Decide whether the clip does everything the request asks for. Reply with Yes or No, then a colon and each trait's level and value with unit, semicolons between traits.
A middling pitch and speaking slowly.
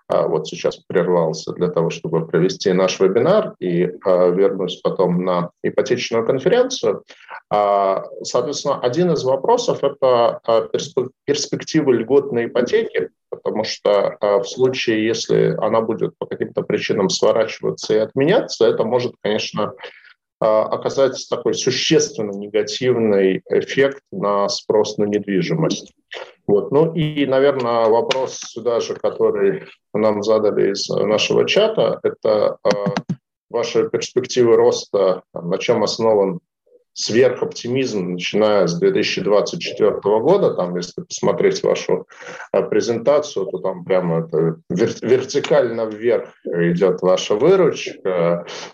No: very high, 390 Hz; slow, 105 wpm